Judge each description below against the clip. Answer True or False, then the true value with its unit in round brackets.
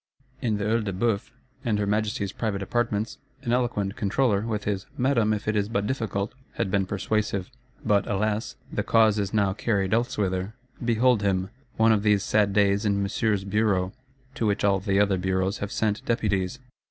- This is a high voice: False (105 Hz)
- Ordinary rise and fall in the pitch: False (2.1 semitones)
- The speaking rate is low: False (180 wpm)